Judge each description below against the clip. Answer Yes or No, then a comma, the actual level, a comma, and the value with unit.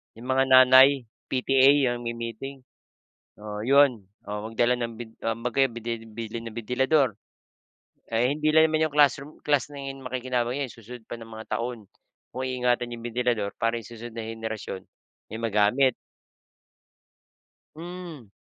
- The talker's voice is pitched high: No, low, 120 Hz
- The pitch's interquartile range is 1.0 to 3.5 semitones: Yes, average, 2.9 semitones